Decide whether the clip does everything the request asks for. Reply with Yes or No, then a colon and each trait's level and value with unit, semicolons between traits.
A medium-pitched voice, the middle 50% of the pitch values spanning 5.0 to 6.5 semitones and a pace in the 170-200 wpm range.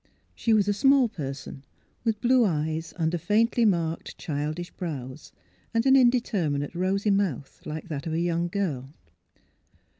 No: medium, 175 Hz; wide, 5.6 semitones; average, 150 wpm